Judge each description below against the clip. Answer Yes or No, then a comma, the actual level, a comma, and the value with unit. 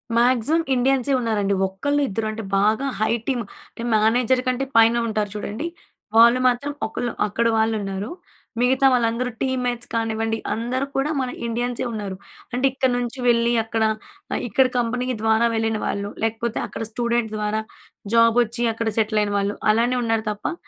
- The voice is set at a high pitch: Yes, high, 230 Hz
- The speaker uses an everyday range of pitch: No, narrow, 2.2 semitones